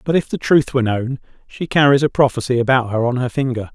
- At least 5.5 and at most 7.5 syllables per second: Yes, 6.2 syllables/s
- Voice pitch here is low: Yes, low, 130 Hz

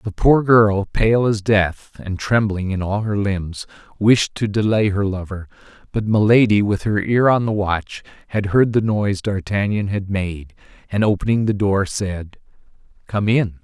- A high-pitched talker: No, low, 105 Hz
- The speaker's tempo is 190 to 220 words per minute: No, average, 170 wpm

